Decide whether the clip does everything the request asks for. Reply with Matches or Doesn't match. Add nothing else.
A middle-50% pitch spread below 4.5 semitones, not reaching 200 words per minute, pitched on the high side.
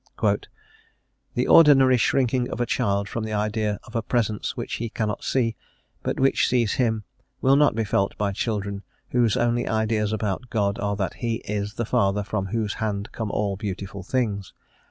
Doesn't match